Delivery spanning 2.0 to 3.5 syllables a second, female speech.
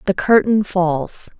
Yes: 3.4 syllables/s; female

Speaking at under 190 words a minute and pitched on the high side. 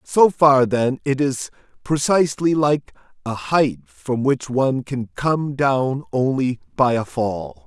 No: average, 150 wpm; low, 135 Hz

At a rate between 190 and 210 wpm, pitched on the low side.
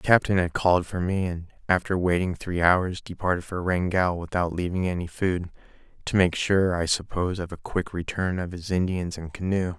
Yes: average, 195 wpm; very low, 90 Hz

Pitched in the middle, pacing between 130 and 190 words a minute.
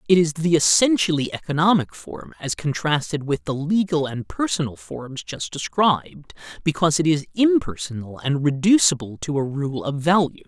Yes: medium, 155 Hz; average, 155 wpm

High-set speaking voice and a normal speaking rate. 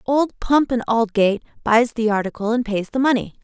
Yes: high, 230 Hz; average, 190 wpm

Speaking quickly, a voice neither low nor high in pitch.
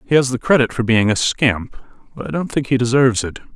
No: fast, 255 wpm; low, 125 Hz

